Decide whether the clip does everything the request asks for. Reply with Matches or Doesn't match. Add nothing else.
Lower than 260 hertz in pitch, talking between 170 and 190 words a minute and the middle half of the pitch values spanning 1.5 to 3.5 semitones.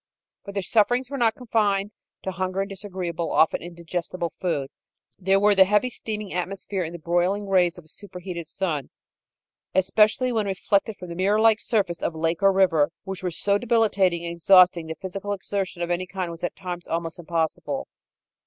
Matches